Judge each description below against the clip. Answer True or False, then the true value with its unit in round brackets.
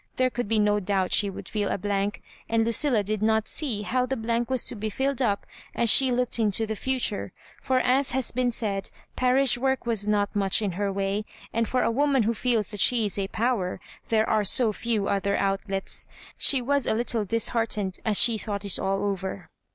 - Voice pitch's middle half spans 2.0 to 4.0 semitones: True (3.4 semitones)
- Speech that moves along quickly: True (220 wpm)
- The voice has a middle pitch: False (220 Hz)